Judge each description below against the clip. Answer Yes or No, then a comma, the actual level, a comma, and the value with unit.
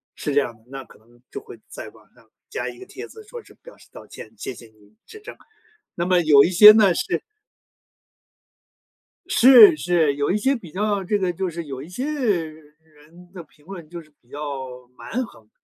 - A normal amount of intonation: No, wide, 6.2 semitones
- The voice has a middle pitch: Yes, medium, 170 Hz